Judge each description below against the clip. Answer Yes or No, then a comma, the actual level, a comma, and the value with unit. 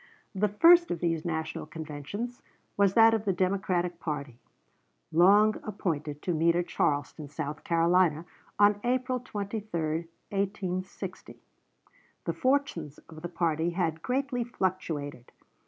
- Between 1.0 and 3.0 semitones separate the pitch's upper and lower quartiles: No, average, 4.6 semitones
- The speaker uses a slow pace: Yes, slow, 125 wpm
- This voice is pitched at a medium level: Yes, medium, 175 Hz